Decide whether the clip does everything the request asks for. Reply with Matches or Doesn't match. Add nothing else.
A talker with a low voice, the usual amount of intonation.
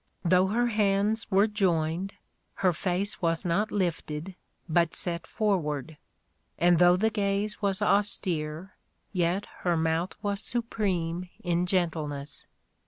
Doesn't match